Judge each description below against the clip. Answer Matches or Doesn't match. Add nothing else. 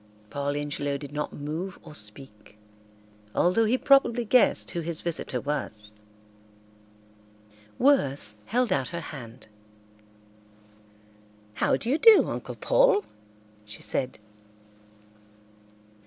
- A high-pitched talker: Doesn't match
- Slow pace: Matches